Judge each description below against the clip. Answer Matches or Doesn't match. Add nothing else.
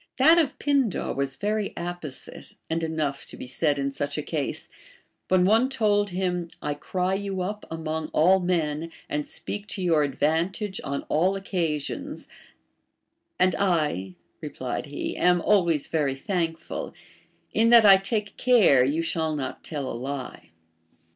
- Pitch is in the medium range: Matches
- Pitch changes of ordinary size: Matches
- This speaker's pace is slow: Doesn't match